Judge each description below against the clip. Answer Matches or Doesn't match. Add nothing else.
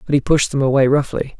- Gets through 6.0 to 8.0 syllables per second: Matches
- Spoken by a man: Matches